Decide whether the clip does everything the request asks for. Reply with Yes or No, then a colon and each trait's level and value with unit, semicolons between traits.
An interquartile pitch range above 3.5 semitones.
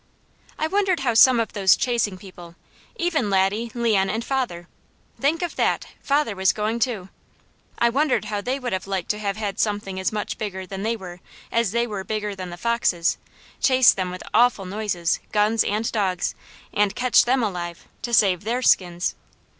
Yes: average, 3.9 semitones